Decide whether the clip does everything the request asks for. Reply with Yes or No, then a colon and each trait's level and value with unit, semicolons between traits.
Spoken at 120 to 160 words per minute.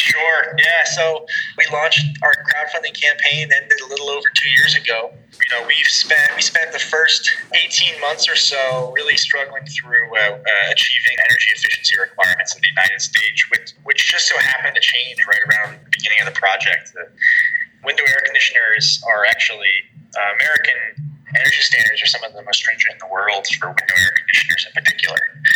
No: average, 185 wpm